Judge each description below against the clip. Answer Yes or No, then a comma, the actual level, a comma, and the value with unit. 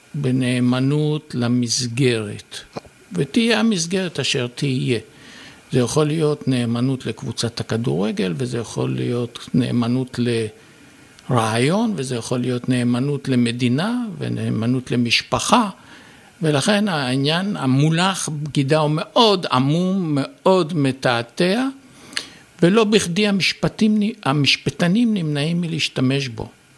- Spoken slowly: Yes, slow, 90 wpm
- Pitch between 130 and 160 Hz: Yes, medium, 140 Hz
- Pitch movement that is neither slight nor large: No, wide, 6.0 semitones